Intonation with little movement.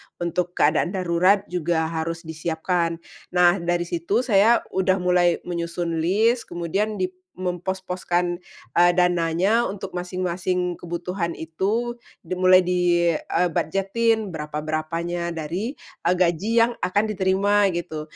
Yes: narrow, 2.0 semitones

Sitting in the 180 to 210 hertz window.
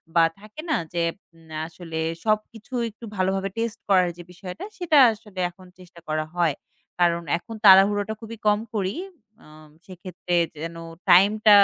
Yes: high, 190 Hz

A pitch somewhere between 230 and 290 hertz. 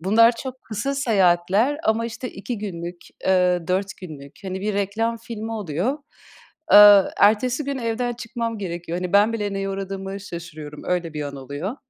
No: high, 200 Hz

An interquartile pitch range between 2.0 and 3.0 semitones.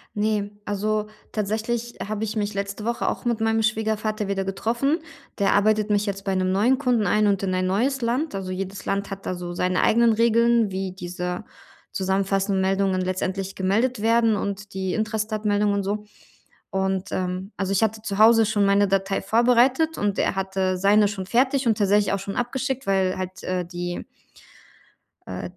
Yes: narrow, 2.5 semitones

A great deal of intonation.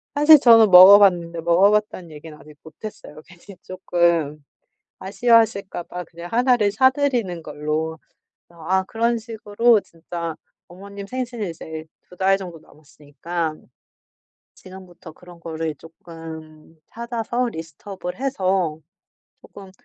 No: average, 4.5 semitones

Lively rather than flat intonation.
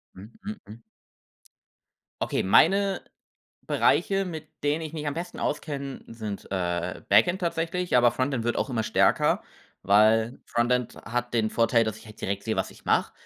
Yes: wide, 6.4 semitones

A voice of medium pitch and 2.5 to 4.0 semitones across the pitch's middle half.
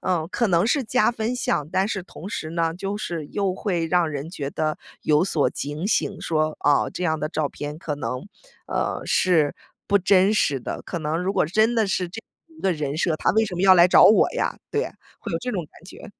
No: medium, 175 Hz; average, 4.4 semitones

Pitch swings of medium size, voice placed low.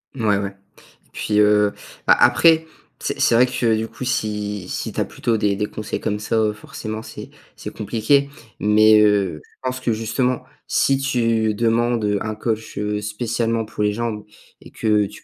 No: narrow, 2.0 semitones; low, 110 Hz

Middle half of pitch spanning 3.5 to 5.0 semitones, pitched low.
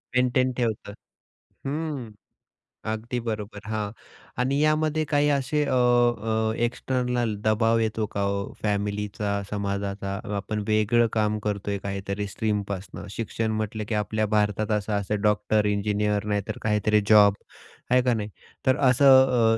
No: average, 2.8 semitones; low, 110 Hz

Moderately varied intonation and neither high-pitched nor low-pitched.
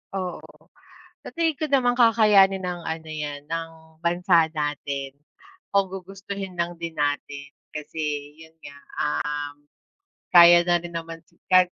Yes: average, 3.7 semitones; medium, 165 Hz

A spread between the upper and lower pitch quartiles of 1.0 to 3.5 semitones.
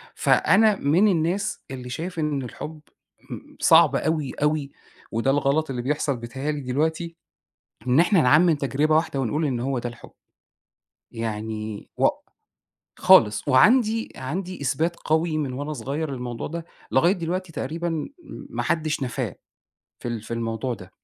No: average, 4.7 semitones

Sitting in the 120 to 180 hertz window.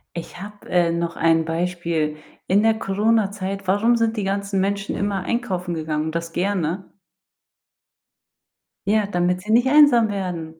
No: high, 195 Hz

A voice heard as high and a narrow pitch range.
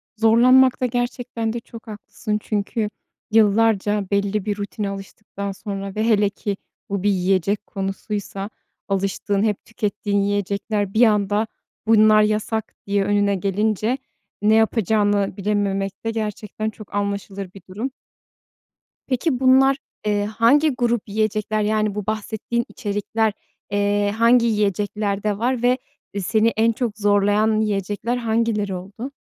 Yes: high, 210 Hz; narrow, 1.8 semitones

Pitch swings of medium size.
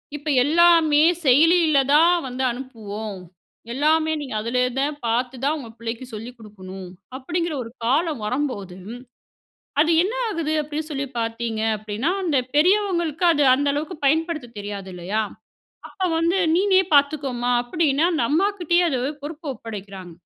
No: wide, 5.9 semitones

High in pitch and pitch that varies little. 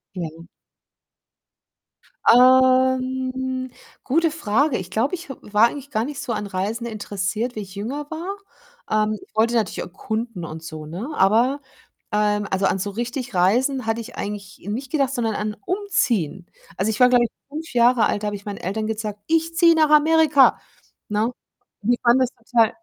No: high, 235 Hz; average, 4.1 semitones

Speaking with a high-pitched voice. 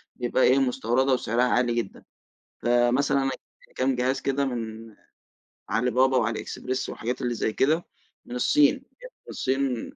No: low, 125 Hz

